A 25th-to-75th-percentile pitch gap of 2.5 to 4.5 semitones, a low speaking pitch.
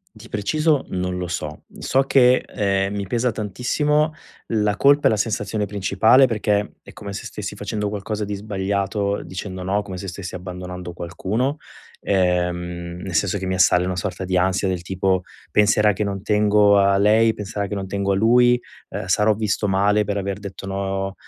No: narrow, 2.1 semitones; low, 100 Hz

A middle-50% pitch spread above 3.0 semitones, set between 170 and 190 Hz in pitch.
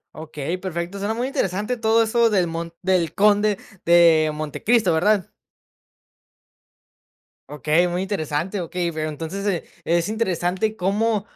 Yes: average, 4.1 semitones; medium, 185 Hz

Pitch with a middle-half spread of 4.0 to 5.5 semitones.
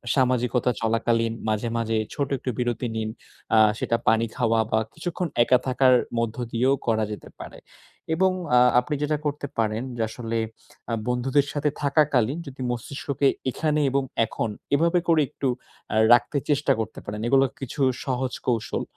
No: average, 3.6 semitones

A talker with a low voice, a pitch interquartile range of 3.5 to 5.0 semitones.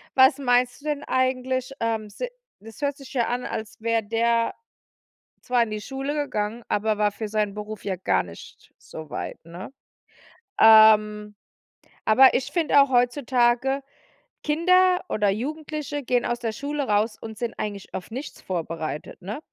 No: high, 235 Hz; average, 4.1 semitones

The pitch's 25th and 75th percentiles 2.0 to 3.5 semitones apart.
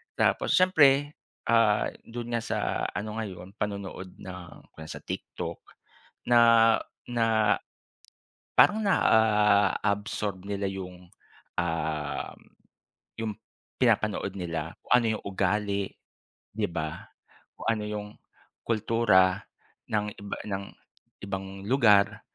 Yes: average, 2.9 semitones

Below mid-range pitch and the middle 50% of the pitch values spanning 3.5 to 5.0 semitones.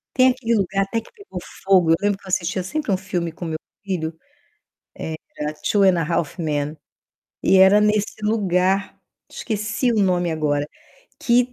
No: high, 190 Hz; average, 4.0 semitones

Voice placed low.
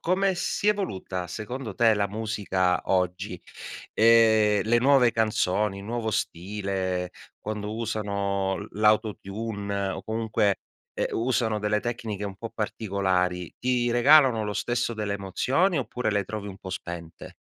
Yes: low, 105 Hz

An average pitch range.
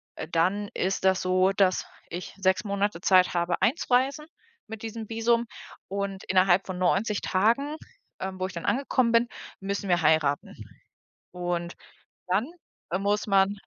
Yes: average, 3.1 semitones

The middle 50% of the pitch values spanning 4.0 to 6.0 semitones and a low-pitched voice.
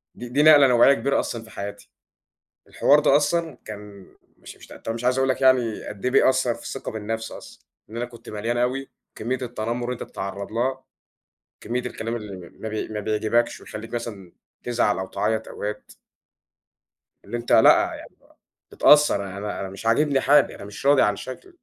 No: average, 3.6 semitones; low, 115 Hz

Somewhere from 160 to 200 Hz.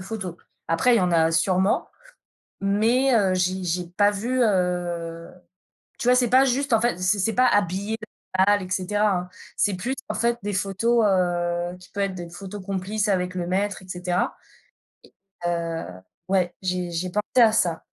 Yes: high, 190 Hz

